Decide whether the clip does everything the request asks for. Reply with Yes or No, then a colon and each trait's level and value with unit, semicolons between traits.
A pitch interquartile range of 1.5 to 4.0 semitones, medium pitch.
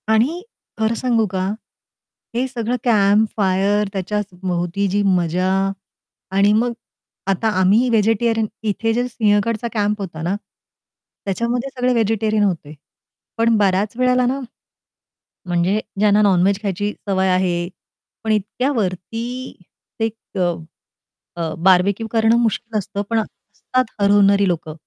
No: average, 3.1 semitones; high, 210 Hz